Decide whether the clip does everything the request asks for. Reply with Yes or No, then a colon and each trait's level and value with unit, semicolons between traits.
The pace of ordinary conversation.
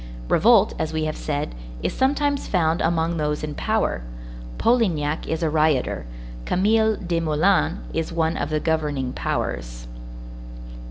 No: slow, 130 wpm